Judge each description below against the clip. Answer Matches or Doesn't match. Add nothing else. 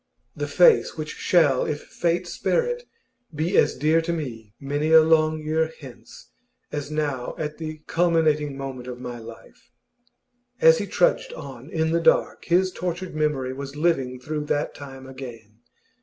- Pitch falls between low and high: Matches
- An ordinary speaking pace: Matches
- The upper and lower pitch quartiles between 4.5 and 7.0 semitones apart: Doesn't match